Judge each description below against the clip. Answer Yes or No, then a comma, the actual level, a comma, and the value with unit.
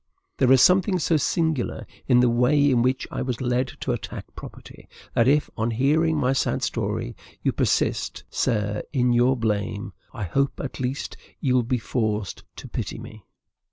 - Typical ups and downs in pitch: Yes, average, 3.0 semitones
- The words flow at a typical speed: Yes, average, 175 wpm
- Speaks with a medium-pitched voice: No, low, 125 Hz